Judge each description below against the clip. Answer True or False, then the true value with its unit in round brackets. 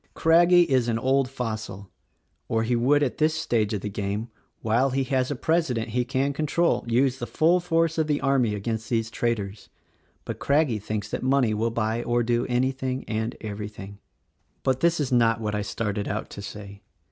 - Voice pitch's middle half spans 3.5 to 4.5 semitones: True (4.0 semitones)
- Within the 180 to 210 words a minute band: True (195 wpm)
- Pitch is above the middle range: False (120 Hz)